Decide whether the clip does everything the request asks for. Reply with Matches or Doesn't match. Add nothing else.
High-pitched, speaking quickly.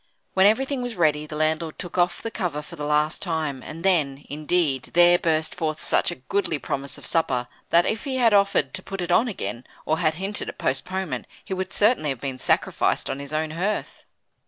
Doesn't match